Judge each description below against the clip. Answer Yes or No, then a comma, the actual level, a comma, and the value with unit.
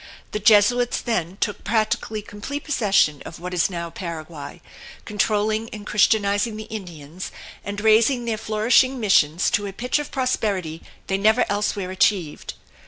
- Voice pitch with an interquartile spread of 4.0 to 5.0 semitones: No, average, 3.4 semitones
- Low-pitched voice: No, high, 205 Hz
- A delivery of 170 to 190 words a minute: No, average, 145 wpm